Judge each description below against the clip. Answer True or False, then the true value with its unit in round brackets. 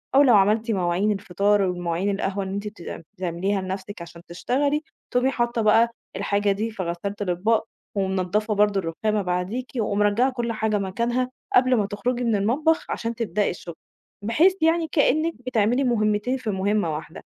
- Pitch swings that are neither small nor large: True (3.7 semitones)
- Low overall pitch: False (210 Hz)